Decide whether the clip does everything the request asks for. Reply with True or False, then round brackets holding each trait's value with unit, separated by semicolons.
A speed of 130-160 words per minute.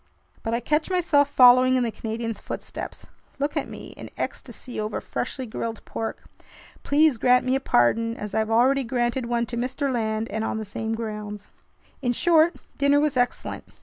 False (175 wpm)